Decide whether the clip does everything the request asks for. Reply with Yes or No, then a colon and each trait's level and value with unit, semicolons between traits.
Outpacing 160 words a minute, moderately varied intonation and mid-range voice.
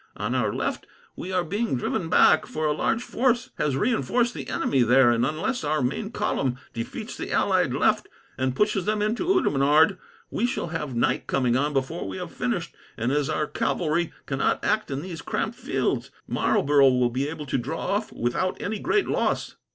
No: average, 190 wpm; wide, 7.3 semitones; medium, 150 Hz